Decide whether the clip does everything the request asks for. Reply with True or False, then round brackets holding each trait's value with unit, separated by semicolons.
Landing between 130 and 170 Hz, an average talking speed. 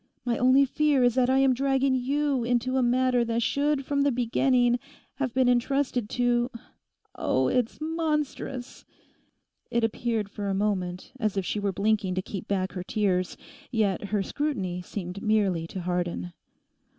False (240 Hz; 160 wpm)